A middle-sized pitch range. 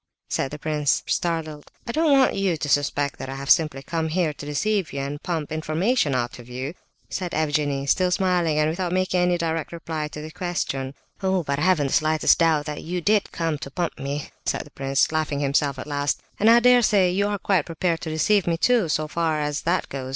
Yes: average, 3.7 semitones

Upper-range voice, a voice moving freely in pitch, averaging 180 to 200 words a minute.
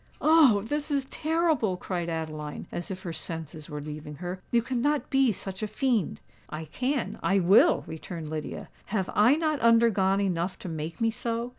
No: high, 195 Hz; wide, 7.1 semitones; average, 170 wpm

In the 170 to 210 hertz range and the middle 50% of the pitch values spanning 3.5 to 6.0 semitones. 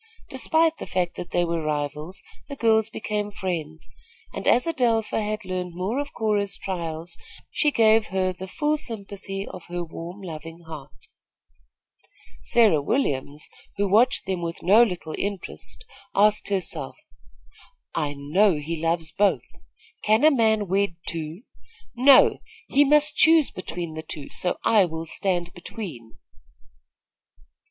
Yes: high, 190 Hz; average, 4.9 semitones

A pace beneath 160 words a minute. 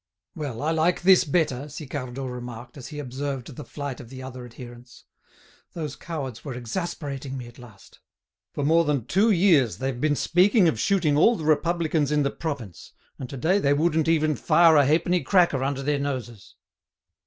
No: average, 180 wpm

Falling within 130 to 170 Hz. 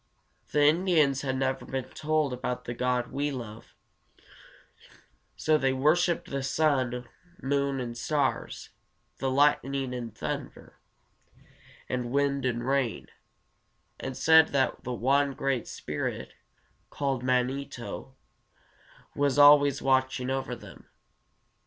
Yes: low, 135 Hz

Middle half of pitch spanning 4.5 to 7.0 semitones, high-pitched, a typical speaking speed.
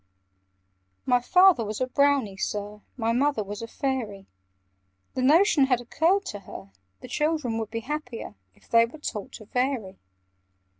Yes: average, 5.0 semitones; high, 245 Hz; average, 155 wpm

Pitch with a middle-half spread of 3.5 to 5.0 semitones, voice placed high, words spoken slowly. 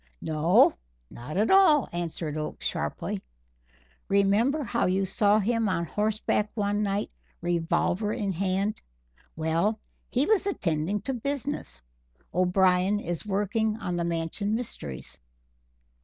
Yes: average, 4.1 semitones; high, 200 Hz; slow, 120 wpm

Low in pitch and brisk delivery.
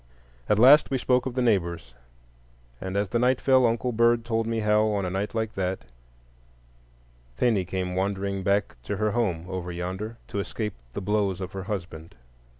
No: low, 105 Hz; average, 175 wpm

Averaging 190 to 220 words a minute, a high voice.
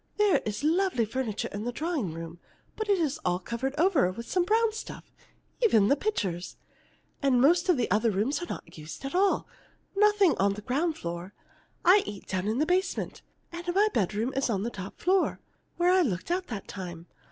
Yes: average, 200 wpm; very high, 265 Hz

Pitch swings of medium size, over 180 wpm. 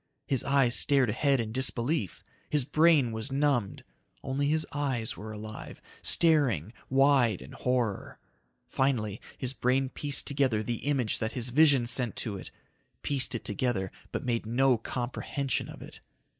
No: average, 3.7 semitones; average, 150 wpm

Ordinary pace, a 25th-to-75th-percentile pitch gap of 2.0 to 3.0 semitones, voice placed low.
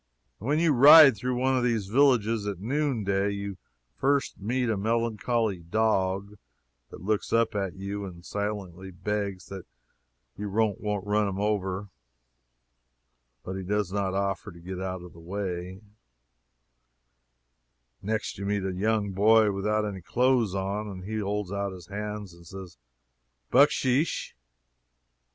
Yes: average, 145 wpm; narrow, 2.6 semitones; low, 100 Hz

